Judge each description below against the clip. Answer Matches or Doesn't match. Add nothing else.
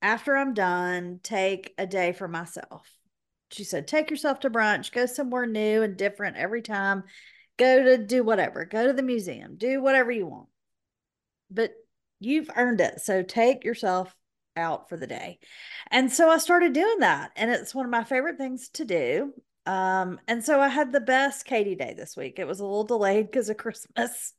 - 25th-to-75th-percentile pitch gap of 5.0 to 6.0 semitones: Matches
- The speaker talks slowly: Doesn't match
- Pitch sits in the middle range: Doesn't match